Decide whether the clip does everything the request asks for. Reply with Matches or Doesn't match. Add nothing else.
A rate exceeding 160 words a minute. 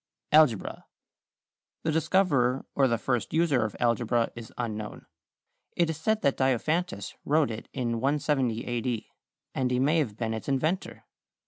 Doesn't match